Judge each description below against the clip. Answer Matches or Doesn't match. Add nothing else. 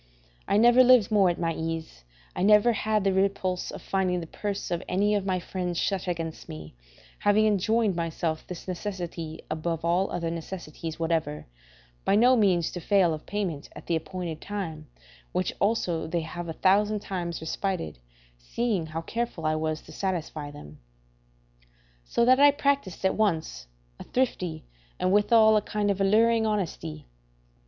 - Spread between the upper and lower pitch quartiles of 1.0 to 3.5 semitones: Doesn't match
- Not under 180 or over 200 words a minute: Doesn't match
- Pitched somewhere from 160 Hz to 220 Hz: Matches